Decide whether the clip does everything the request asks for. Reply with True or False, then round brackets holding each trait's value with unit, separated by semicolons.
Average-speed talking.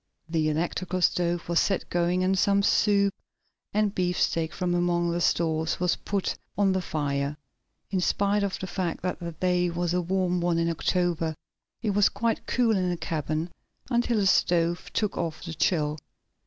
True (175 wpm)